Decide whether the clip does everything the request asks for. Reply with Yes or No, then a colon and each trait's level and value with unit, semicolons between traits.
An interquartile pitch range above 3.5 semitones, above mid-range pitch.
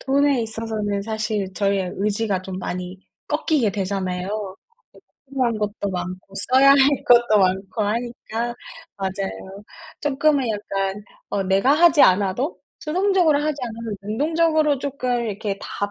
Yes: wide, 5.5 semitones; high, 215 Hz